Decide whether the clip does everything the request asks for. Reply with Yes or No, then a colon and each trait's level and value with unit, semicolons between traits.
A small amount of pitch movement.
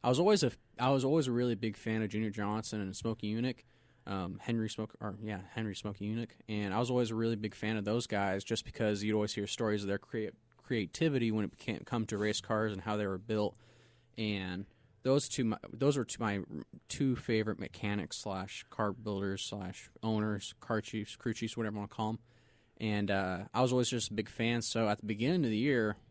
Yes: narrow, 2.0 semitones